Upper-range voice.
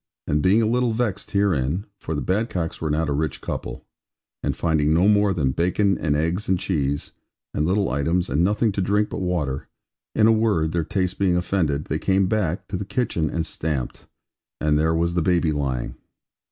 No: very low, 85 Hz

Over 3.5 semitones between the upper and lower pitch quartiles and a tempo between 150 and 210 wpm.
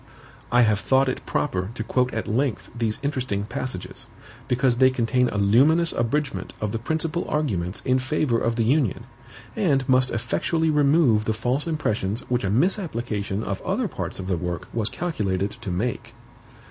Yes: average, 4.6 semitones; average, 170 wpm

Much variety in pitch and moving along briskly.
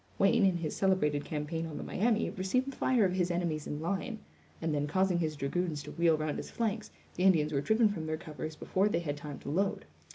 No: average, 4.1 semitones; fast, 230 wpm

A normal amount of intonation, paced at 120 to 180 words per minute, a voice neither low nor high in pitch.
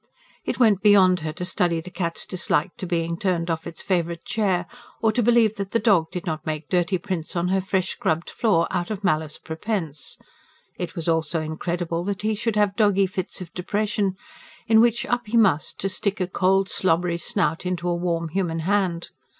No: average, 3.3 semitones; average, 200 wpm; medium, 180 Hz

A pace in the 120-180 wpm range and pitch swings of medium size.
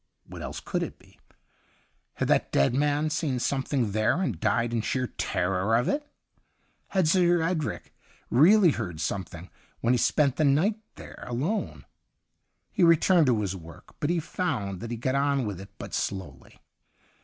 No: average, 175 wpm; wide, 7.4 semitones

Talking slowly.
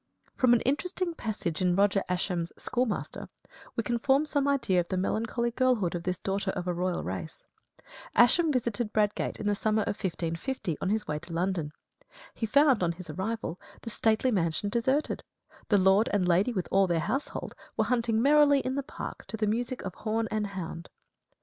No: average, 190 wpm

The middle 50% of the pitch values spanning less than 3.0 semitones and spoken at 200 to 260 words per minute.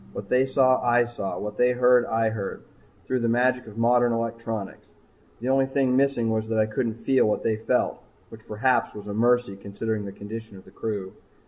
Yes: narrow, 2.4 semitones; fast, 205 wpm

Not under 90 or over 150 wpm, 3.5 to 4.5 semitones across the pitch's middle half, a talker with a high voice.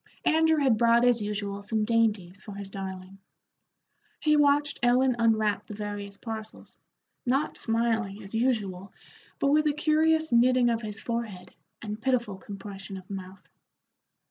Yes: average, 145 wpm; average, 3.9 semitones; high, 225 Hz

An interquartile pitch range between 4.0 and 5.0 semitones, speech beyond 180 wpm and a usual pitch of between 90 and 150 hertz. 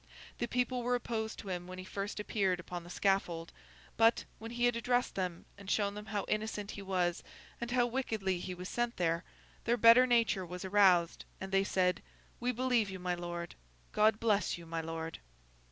No: average, 4.3 semitones; average, 195 wpm; high, 200 Hz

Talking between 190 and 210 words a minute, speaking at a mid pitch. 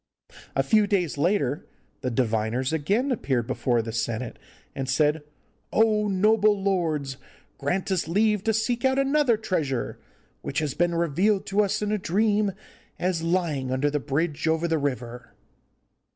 No: average, 150 wpm; medium, 170 Hz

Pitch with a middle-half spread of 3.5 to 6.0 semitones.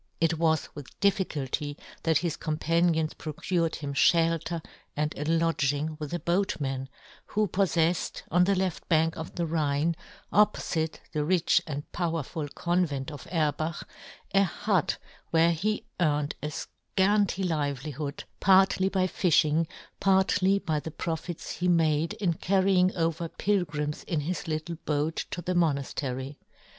No: average, 3.1 semitones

